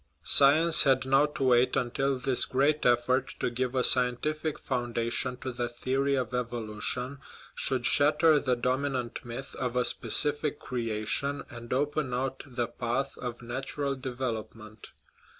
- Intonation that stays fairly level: Yes, narrow, 2.3 semitones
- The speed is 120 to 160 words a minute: Yes, average, 150 wpm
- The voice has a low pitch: Yes, low, 130 Hz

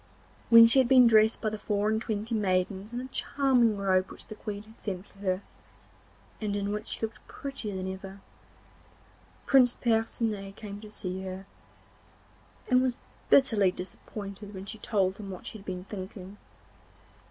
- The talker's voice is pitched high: Yes, high, 210 Hz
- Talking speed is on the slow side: No, average, 170 wpm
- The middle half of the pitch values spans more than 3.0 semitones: No, narrow, 2.6 semitones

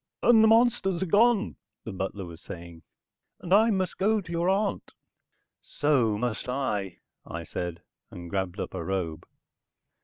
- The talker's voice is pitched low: Yes, low, 125 Hz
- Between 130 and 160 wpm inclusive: Yes, average, 155 wpm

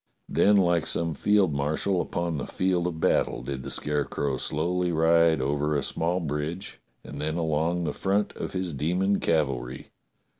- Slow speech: No, average, 165 wpm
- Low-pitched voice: Yes, very low, 80 Hz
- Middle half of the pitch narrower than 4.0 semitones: Yes, average, 3.3 semitones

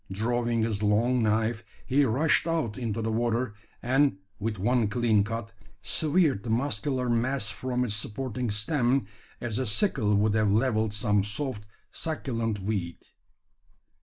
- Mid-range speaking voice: No, low, 115 Hz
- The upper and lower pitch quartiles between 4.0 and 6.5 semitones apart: No, average, 3.3 semitones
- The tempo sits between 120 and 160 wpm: Yes, average, 140 wpm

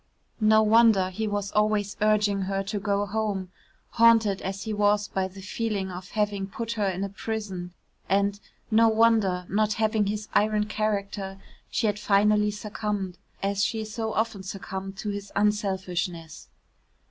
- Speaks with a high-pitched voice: Yes, high, 205 Hz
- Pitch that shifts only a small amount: Yes, narrow, 1.7 semitones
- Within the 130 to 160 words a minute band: Yes, average, 155 wpm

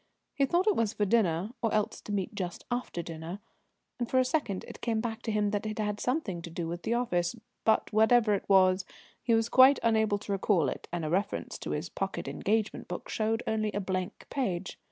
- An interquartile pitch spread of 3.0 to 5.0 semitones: Yes, average, 3.7 semitones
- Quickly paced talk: Yes, fast, 220 wpm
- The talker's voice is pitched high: Yes, high, 210 Hz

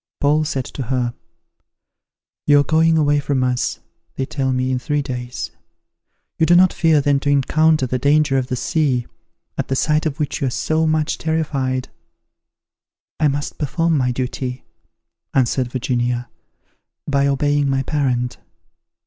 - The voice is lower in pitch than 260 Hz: Yes, medium, 140 Hz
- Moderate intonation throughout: Yes, average, 3.0 semitones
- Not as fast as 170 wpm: Yes, average, 155 wpm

